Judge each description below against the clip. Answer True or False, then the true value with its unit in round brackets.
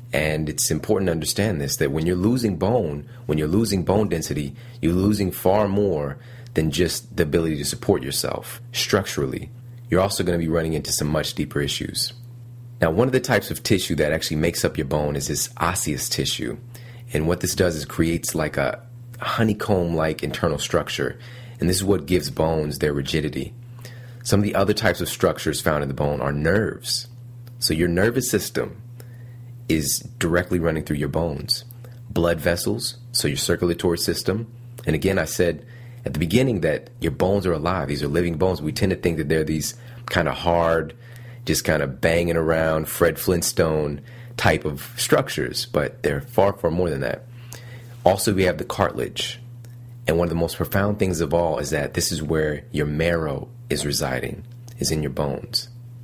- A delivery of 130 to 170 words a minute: False (185 wpm)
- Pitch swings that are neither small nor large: False (7.1 semitones)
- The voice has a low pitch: True (95 Hz)